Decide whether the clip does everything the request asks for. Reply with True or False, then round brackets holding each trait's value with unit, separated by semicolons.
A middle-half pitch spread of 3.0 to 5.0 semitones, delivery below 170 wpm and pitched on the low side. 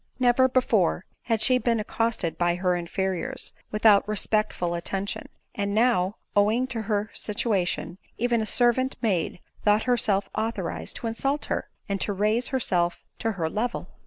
False (3.7 semitones; 155 wpm; 215 Hz)